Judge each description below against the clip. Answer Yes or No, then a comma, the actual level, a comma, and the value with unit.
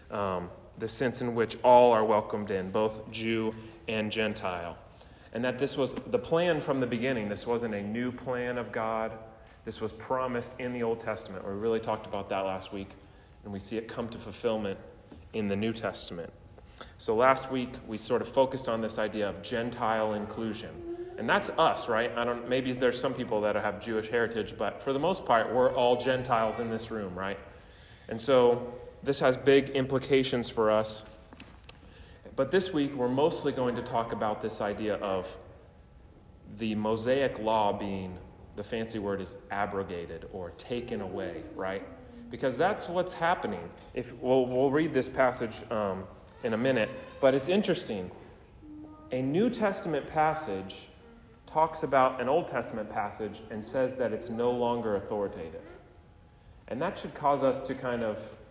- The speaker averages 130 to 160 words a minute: No, average, 170 wpm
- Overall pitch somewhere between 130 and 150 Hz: No, low, 115 Hz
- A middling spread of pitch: Yes, average, 3.8 semitones